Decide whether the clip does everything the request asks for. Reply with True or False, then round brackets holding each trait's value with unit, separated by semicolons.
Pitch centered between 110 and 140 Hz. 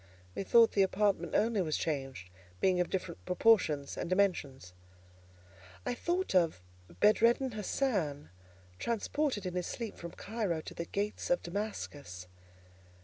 False (185 Hz)